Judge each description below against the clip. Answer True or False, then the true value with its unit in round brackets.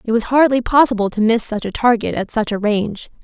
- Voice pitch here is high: True (225 Hz)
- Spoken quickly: True (240 wpm)